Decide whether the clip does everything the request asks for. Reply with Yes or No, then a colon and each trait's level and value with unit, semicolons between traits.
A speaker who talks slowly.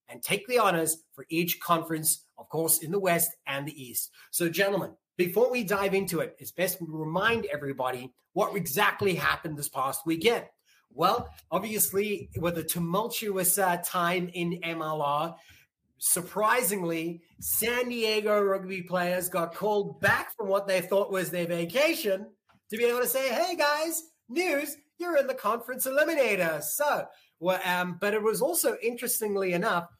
No: average, 160 wpm